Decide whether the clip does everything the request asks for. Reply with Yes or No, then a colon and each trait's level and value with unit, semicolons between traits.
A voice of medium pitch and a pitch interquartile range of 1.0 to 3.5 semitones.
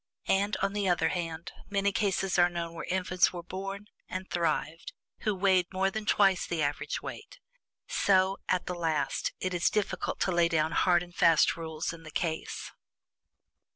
Yes: medium, 180 Hz; narrow, 2.6 semitones